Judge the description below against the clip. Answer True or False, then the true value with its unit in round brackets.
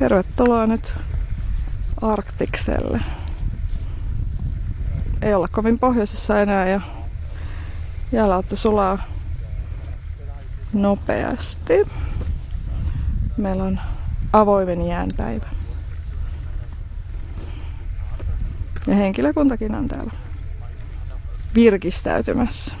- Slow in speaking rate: True (55 wpm)